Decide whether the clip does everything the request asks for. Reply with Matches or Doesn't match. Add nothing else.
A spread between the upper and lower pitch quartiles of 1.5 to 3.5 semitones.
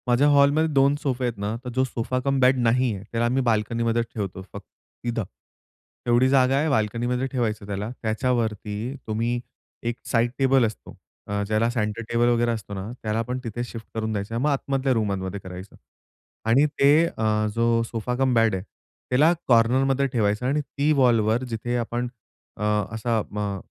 Matches